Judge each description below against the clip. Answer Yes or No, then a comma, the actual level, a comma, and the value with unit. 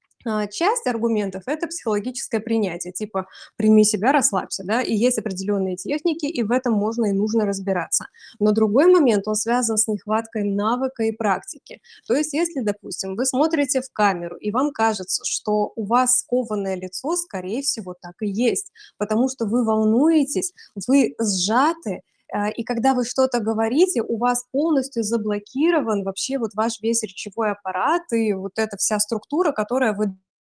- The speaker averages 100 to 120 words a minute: No, fast, 160 wpm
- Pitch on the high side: Yes, high, 225 Hz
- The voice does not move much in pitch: No, average, 3.9 semitones